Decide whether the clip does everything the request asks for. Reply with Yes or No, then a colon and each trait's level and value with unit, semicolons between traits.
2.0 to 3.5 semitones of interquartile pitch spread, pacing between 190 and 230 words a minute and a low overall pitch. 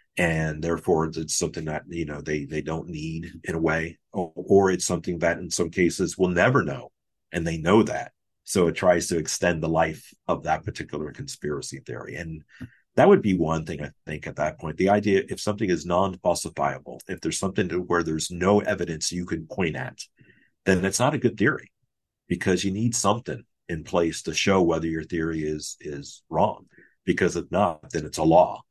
Yes: narrow, 2.4 semitones; fast, 205 wpm; very low, 85 Hz